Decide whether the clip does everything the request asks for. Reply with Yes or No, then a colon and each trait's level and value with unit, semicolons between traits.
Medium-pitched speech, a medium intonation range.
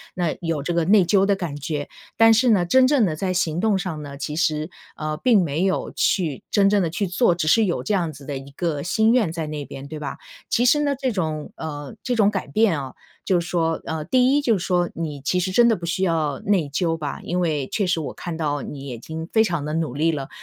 Yes: medium, 170 Hz; average, 4.5 semitones